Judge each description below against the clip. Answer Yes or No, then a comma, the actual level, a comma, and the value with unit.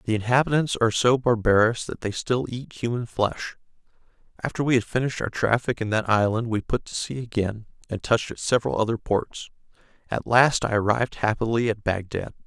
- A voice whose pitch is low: Yes, low, 115 Hz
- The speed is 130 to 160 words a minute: No, average, 185 wpm